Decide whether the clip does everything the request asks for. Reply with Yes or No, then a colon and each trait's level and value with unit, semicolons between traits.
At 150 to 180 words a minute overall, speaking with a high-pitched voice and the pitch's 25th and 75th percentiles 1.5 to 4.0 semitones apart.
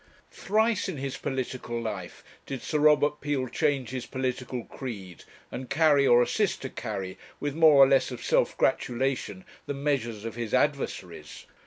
No: average, 160 wpm; low, 130 Hz; average, 3.6 semitones